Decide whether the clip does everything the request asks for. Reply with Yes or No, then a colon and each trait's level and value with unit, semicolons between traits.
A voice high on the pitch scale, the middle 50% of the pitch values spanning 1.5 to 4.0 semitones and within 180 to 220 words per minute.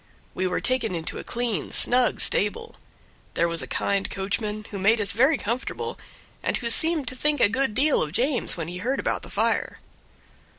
No: high, 230 Hz; average, 5.2 semitones; average, 195 wpm